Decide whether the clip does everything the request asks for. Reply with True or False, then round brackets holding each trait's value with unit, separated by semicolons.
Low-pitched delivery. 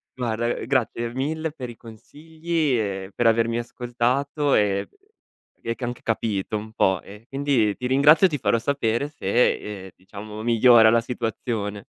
True (120 Hz)